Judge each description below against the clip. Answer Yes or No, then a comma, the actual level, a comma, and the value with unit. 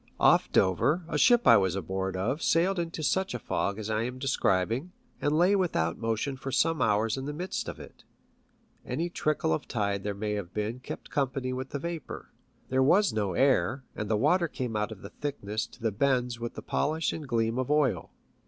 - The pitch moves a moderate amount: No, wide, 6.1 semitones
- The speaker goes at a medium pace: No, fast, 210 wpm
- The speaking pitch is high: No, low, 130 Hz